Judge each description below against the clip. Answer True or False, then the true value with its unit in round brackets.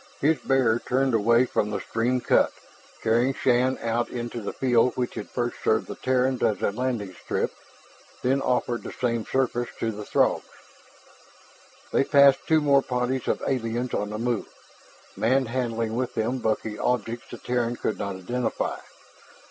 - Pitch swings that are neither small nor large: False (2.1 semitones)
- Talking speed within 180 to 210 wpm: False (160 wpm)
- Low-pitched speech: True (120 Hz)